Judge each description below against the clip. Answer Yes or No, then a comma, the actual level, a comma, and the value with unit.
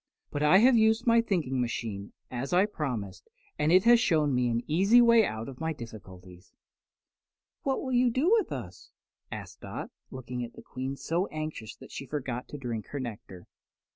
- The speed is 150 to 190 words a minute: Yes, average, 185 wpm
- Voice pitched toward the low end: No, medium, 145 Hz